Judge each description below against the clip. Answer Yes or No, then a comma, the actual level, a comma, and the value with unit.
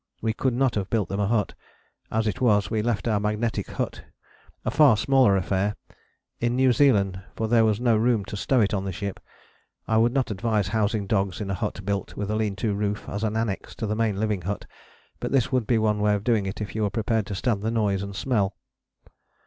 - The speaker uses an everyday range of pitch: No, narrow, 2.2 semitones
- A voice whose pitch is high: No, low, 105 Hz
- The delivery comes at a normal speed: No, fast, 235 wpm